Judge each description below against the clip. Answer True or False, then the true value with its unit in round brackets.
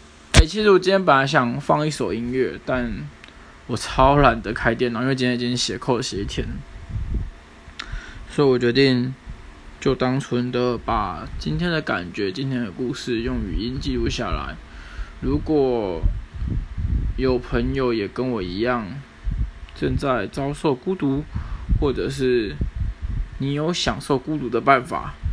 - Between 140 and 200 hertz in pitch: False (125 Hz)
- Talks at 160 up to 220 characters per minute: True (210 characters per minute)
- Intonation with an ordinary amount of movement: False (6.4 semitones)